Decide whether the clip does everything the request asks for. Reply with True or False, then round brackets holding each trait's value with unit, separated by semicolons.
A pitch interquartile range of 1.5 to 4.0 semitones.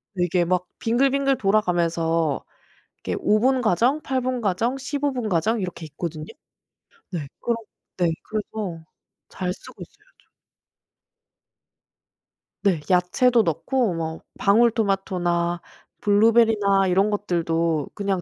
False (5.1 semitones)